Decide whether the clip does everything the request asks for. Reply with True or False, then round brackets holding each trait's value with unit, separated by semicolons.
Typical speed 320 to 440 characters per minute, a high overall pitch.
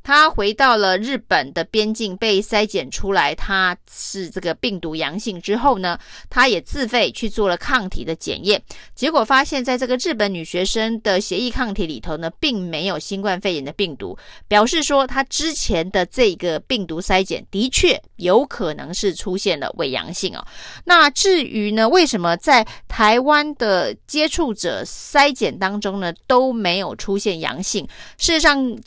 False (255 characters per minute; 210 Hz)